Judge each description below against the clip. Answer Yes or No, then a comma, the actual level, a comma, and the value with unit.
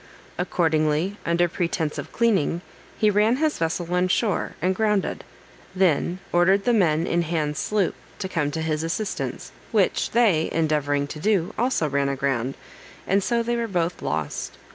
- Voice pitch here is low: No, medium, 175 Hz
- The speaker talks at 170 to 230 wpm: No, average, 160 wpm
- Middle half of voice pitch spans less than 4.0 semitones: No, average, 4.7 semitones